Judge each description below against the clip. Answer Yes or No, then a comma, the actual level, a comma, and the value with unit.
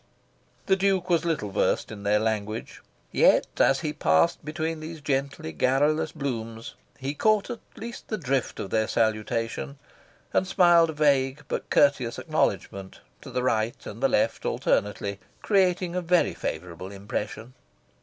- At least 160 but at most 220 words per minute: No, average, 150 wpm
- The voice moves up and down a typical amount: No, wide, 7.2 semitones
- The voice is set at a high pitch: No, low, 135 Hz